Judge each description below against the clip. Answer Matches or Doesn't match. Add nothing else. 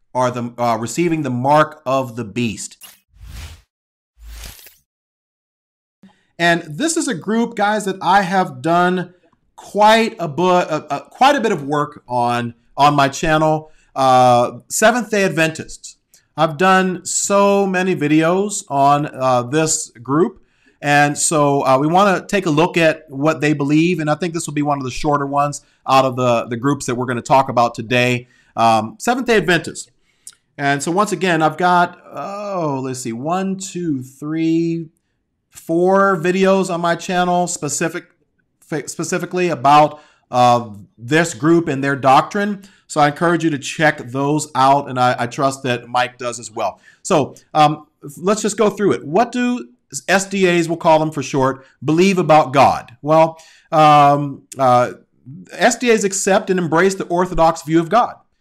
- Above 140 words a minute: Matches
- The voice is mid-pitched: Matches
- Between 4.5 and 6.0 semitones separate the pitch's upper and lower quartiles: Matches